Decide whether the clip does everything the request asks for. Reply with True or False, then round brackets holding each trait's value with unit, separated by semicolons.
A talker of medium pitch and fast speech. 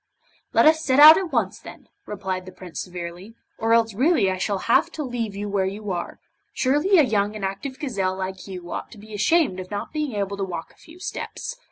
False (205 Hz; 225 wpm)